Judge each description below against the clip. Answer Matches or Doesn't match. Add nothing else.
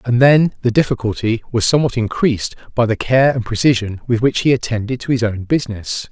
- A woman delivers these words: Doesn't match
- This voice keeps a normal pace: Matches